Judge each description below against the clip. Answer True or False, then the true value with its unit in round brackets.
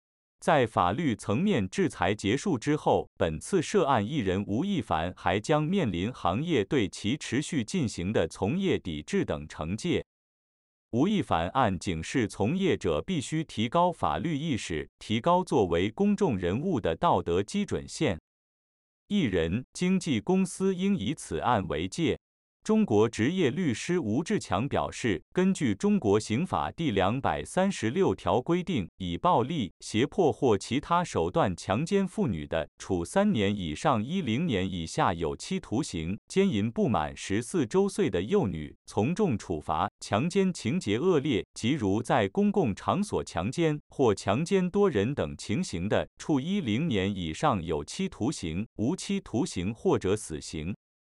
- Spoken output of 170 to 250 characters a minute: True (230 characters per minute)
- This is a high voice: False (150 Hz)